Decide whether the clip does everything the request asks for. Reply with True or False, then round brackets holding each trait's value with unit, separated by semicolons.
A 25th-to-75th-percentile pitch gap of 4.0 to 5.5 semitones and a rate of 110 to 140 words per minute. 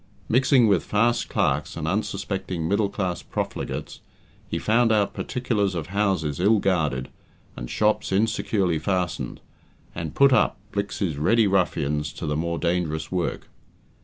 True (4.7 semitones; 135 wpm)